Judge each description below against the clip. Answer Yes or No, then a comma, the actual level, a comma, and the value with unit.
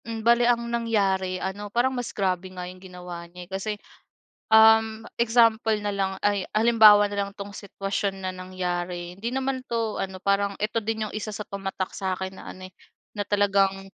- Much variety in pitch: No, average, 2.8 semitones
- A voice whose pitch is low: No, high, 200 Hz